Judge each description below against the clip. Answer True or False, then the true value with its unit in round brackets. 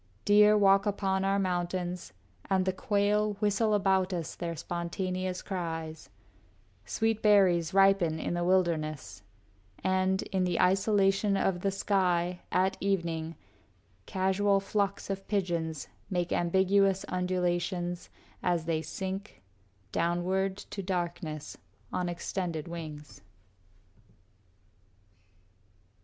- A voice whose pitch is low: False (185 Hz)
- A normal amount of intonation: False (2.2 semitones)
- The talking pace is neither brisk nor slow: False (105 wpm)